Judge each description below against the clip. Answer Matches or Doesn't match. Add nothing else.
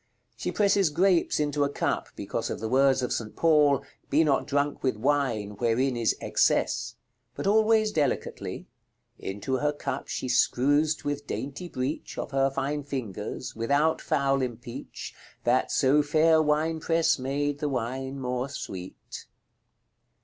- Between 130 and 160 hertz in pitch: Matches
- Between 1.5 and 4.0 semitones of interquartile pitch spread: Matches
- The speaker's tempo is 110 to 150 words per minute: Matches